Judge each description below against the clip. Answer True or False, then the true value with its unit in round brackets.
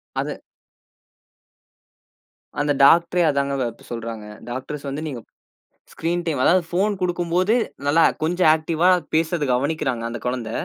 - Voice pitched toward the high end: False (155 Hz)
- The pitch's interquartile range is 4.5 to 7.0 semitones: True (5.1 semitones)